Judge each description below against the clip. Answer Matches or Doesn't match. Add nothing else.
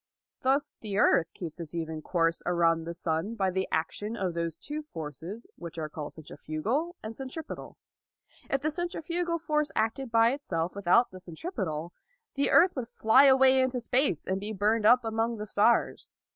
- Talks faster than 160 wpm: Matches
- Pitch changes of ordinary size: Doesn't match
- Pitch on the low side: Doesn't match